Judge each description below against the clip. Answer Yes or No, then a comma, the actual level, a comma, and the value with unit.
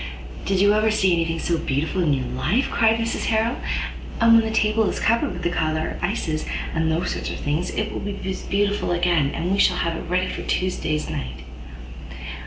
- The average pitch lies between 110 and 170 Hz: No, medium, 180 Hz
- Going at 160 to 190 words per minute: No, fast, 205 wpm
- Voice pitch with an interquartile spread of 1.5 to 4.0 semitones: No, average, 4.9 semitones